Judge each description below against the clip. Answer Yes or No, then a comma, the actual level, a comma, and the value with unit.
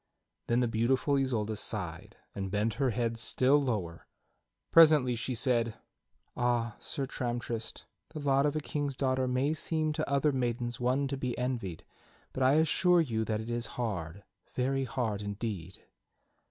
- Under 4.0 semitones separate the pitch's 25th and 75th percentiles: Yes, average, 3.5 semitones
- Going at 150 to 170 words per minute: Yes, average, 155 wpm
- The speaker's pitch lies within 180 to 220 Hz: No, low, 125 Hz